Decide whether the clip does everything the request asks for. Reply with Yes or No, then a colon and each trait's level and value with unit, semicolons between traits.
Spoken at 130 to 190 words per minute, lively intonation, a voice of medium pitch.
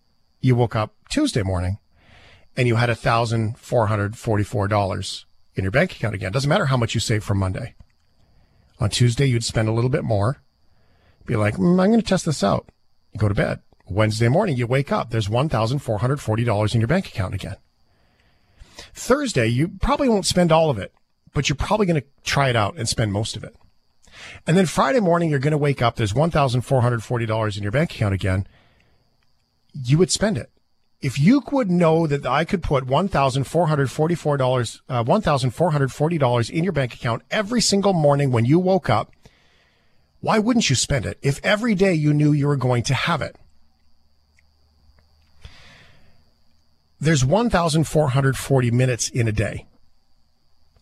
No: average, 185 wpm; wide, 6.6 semitones; low, 125 Hz